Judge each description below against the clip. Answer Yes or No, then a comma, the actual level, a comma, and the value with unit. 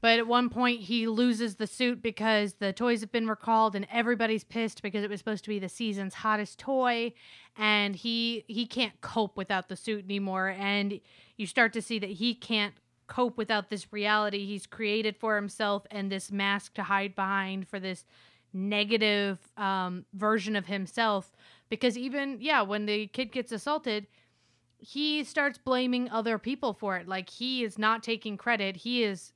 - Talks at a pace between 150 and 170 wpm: No, average, 180 wpm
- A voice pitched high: Yes, high, 215 Hz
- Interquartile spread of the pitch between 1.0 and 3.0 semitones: Yes, narrow, 2.6 semitones